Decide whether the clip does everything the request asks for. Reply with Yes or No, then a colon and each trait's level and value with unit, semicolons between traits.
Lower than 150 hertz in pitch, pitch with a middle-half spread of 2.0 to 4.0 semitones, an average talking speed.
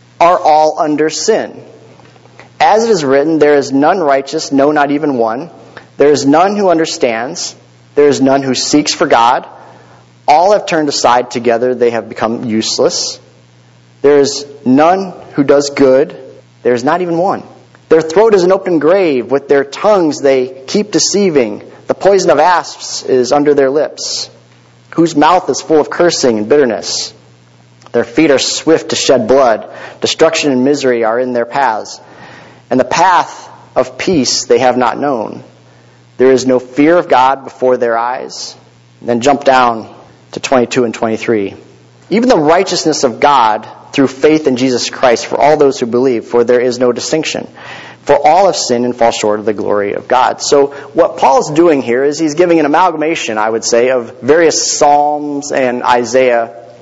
No: low, 135 Hz; average, 4.7 semitones; average, 175 wpm